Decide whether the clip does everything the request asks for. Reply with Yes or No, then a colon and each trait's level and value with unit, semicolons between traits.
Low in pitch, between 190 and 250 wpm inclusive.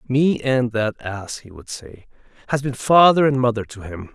Yes: low, 125 Hz; fast, 205 wpm